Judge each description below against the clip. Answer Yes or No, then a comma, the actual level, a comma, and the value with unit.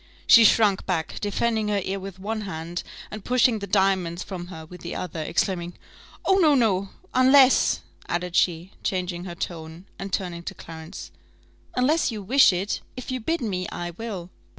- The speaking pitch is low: No, high, 190 Hz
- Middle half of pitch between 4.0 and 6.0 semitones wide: Yes, average, 4.3 semitones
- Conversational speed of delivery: Yes, average, 175 wpm